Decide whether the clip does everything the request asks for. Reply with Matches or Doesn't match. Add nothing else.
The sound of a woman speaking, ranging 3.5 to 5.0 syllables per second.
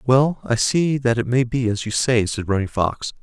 Doesn't match